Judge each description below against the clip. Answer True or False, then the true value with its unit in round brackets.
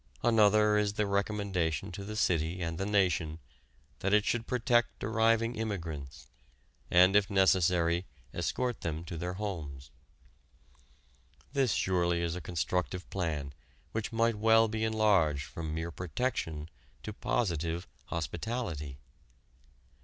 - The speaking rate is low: True (125 wpm)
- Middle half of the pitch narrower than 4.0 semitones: False (4.5 semitones)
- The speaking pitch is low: True (95 Hz)